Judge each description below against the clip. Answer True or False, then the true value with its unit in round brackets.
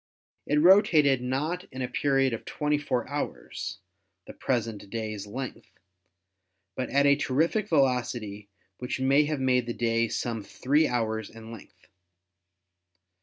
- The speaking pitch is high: False (130 Hz)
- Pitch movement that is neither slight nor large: True (3.9 semitones)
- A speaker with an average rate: False (130 wpm)